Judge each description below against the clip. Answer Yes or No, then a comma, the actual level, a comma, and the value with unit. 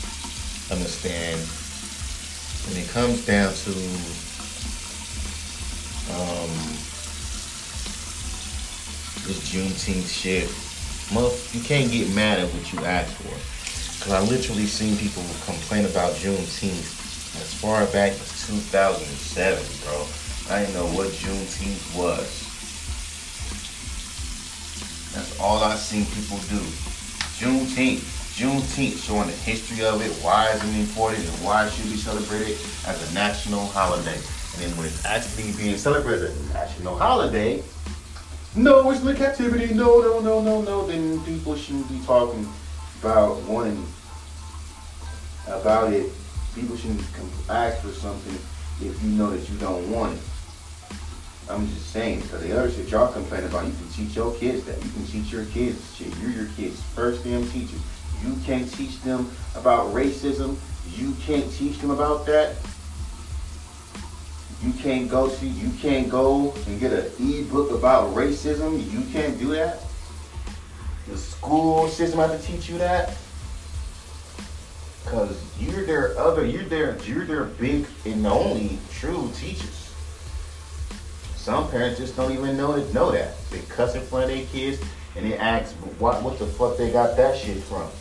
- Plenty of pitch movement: Yes, wide, 6.3 semitones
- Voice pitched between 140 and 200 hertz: No, very low, 85 Hz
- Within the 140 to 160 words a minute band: Yes, average, 150 wpm